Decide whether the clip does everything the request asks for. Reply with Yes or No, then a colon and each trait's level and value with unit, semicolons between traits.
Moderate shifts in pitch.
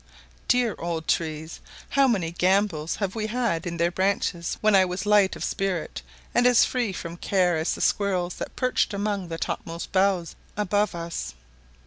Yes: average, 3.6 semitones